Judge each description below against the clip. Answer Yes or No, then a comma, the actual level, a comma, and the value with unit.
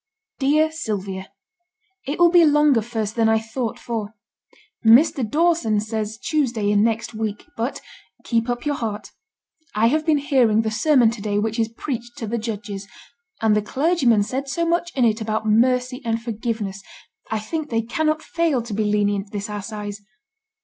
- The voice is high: Yes, high, 225 Hz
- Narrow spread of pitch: No, average, 4.3 semitones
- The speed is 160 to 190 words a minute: Yes, average, 170 wpm